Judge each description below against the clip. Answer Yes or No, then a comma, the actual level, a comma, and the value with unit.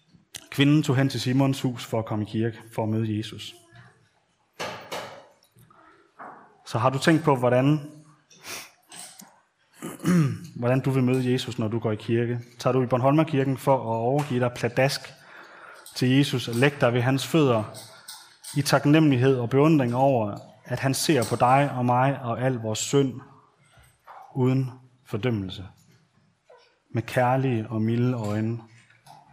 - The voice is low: Yes, low, 130 Hz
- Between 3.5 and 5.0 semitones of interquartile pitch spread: No, average, 2.7 semitones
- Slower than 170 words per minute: Yes, slow, 145 wpm